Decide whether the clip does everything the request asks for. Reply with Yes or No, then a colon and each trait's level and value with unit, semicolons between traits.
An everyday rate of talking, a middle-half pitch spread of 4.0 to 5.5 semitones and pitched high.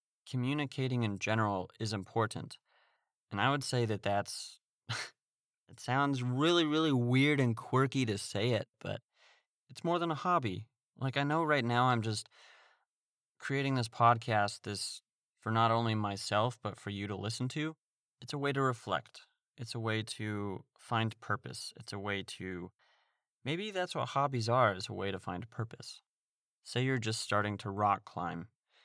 No: average, 170 wpm; average, 4.5 semitones; low, 120 Hz